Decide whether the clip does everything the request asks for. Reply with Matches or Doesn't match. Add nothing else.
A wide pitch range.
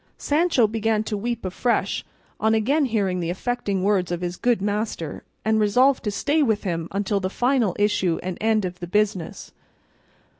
Doesn't match